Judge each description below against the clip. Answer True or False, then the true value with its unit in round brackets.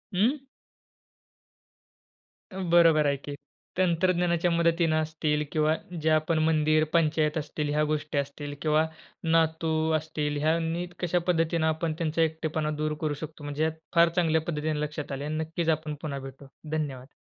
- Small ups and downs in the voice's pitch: True (1.5 semitones)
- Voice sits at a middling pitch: True (155 Hz)